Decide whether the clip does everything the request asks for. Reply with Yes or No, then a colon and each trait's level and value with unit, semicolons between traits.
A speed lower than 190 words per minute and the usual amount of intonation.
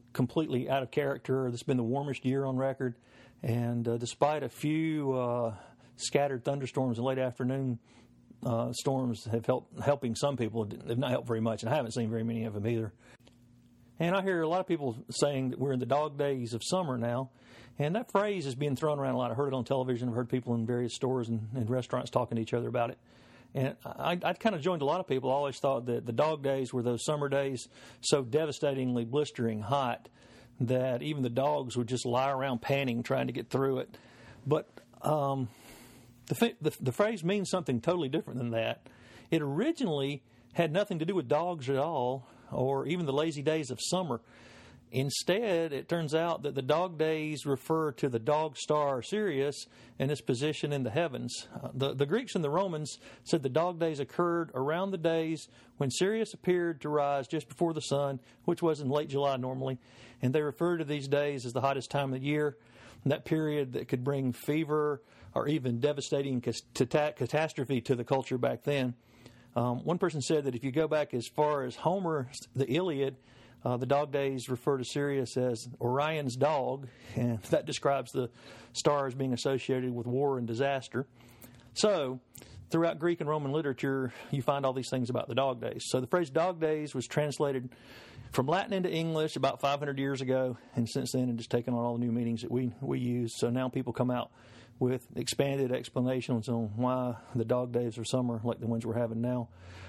No: fast, 205 wpm; average, 3.5 semitones